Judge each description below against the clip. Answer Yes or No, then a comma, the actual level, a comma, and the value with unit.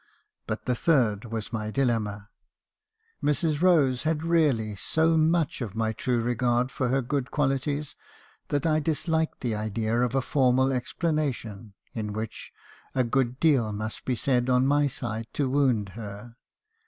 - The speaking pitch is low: Yes, low, 125 Hz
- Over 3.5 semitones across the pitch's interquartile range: Yes, average, 4.5 semitones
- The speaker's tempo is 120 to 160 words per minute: Yes, average, 155 wpm